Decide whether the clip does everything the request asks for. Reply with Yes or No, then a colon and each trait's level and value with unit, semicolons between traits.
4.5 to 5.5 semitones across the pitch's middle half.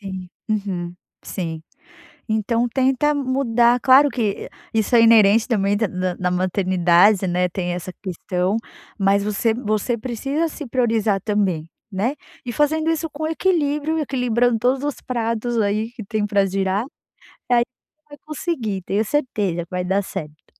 Yes: average, 4.9 semitones